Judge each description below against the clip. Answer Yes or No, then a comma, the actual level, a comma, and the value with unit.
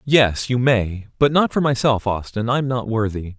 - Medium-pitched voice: No, low, 115 Hz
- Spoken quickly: No, average, 175 wpm